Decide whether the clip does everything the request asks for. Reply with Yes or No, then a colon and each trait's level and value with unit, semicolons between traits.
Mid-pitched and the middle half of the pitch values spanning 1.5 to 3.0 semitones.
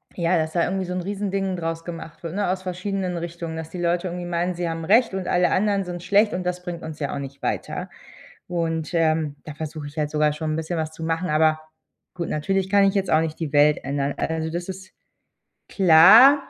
Yes: medium, 170 Hz; average, 2.7 semitones